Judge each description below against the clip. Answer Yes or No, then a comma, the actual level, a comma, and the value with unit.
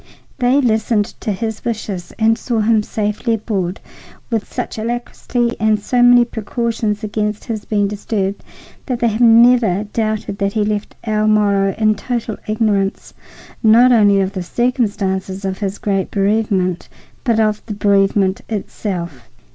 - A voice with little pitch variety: Yes, narrow, 2.3 semitones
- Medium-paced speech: Yes, average, 150 wpm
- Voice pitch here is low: No, high, 215 Hz